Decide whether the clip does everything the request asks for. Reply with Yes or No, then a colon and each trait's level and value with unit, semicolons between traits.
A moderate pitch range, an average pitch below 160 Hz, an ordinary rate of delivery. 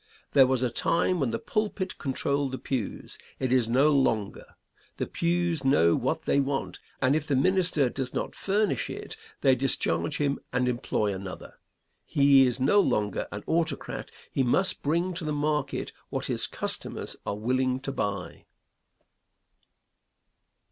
Yes: average, 3.7 semitones; low, 135 Hz; average, 155 wpm